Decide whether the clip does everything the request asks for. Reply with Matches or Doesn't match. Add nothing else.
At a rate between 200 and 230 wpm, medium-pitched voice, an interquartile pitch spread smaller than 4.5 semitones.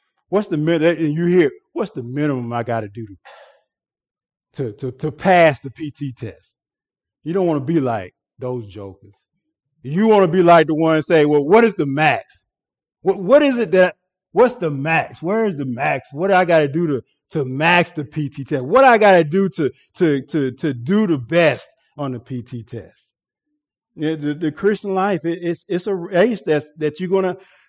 Doesn't match